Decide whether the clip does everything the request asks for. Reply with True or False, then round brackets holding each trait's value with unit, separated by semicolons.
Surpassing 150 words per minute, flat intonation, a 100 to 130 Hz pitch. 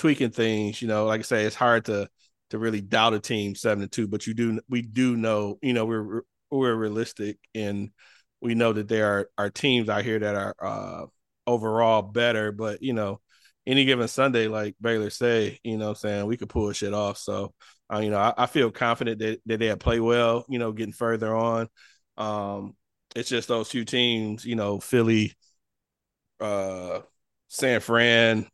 True (190 wpm; 1.8 semitones; 110 Hz)